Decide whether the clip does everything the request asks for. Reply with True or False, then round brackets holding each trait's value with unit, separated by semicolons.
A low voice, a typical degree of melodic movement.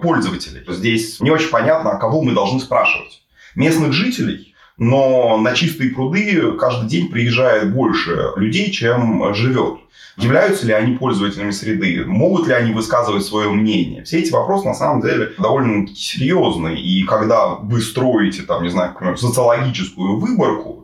True (120 Hz; 4.2 semitones)